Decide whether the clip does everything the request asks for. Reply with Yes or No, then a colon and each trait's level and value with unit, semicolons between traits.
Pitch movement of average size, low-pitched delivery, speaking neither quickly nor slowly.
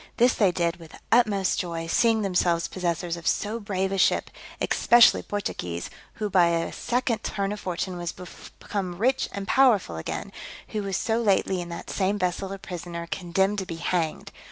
No: average, 3.3 semitones; high, 190 Hz; average, 180 wpm